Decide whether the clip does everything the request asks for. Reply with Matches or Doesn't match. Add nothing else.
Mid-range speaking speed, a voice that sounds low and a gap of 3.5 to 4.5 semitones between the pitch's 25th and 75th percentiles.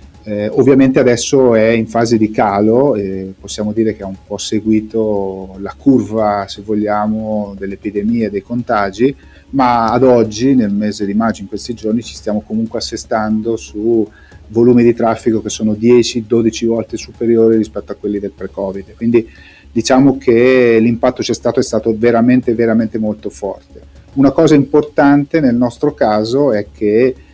Doesn't match